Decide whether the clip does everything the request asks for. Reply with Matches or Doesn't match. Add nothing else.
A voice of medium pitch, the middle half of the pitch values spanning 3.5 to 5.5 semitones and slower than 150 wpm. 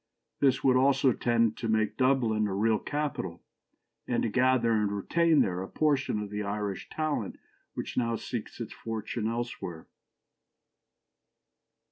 Doesn't match